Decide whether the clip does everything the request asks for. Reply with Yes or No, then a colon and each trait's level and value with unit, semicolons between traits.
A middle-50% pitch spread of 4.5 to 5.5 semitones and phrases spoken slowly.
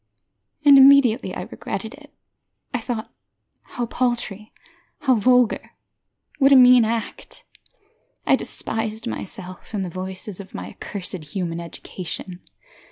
Yes: average, 4.9 semitones; slow, 120 wpm